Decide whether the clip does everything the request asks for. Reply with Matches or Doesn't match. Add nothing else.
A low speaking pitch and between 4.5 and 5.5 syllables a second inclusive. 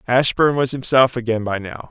Matches